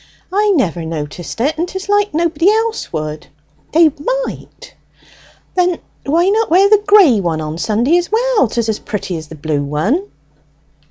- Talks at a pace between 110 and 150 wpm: No, average, 165 wpm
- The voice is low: No, very high, 305 Hz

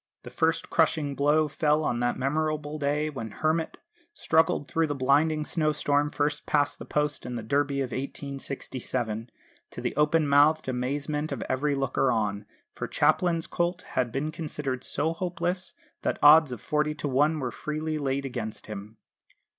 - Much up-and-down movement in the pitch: No, average, 2.9 semitones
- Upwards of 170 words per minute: No, average, 165 wpm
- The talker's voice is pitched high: No, medium, 145 Hz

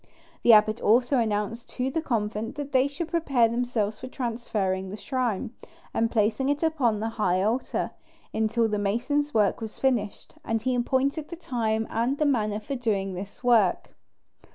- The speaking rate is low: No, average, 170 wpm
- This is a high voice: Yes, high, 230 Hz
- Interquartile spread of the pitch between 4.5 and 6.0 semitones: No, average, 3.7 semitones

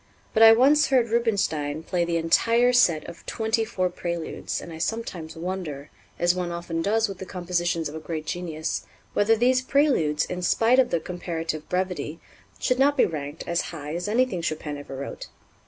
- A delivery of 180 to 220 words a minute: Yes, average, 185 wpm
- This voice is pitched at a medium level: Yes, medium, 175 Hz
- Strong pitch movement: Yes, wide, 5.7 semitones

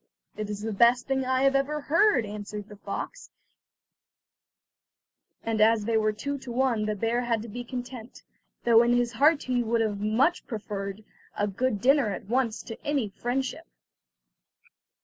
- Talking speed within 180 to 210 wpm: No, average, 170 wpm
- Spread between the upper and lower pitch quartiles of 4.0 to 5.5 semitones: No, average, 3.5 semitones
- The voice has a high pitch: Yes, high, 235 Hz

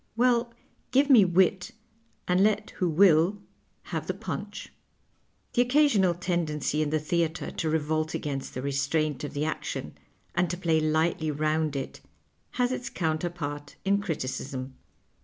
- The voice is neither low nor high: Yes, medium, 160 Hz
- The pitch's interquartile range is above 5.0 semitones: No, average, 4.1 semitones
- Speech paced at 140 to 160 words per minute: Yes, average, 145 wpm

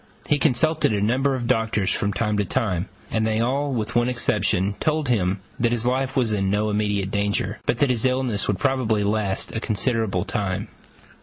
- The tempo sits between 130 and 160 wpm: No, average, 190 wpm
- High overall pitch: No, low, 110 Hz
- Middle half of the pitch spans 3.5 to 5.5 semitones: Yes, average, 3.8 semitones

